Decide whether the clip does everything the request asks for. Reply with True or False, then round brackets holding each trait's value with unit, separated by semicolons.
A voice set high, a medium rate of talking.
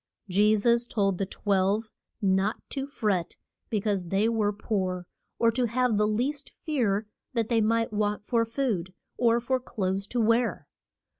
True (215 Hz; 160 wpm)